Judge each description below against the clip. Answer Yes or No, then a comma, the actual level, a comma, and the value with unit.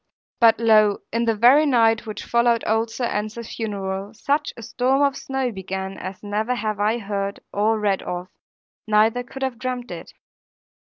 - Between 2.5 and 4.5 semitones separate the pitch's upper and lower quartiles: Yes, average, 3.0 semitones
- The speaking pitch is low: No, high, 225 Hz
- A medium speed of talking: Yes, average, 170 wpm